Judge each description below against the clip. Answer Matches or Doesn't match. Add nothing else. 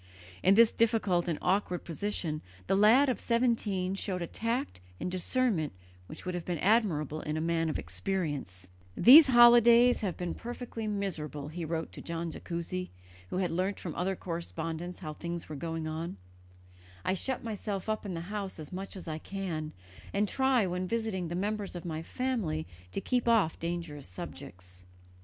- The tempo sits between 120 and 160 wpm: Doesn't match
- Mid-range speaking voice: Matches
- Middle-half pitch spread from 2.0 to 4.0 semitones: Doesn't match